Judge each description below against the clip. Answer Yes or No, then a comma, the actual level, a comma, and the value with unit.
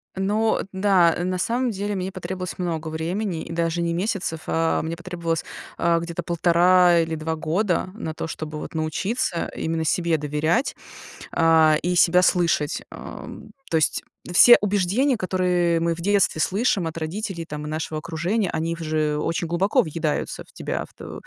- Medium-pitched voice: Yes, medium, 170 Hz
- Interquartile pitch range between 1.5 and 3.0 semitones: Yes, narrow, 2.6 semitones